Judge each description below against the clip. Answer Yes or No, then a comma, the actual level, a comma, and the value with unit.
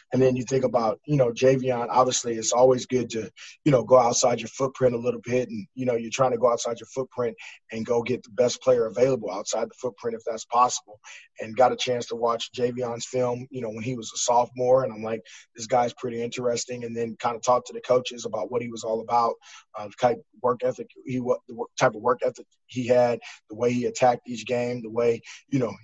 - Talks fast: Yes, fast, 245 wpm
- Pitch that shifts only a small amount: Yes, narrow, 1.4 semitones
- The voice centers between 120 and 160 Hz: Yes, low, 125 Hz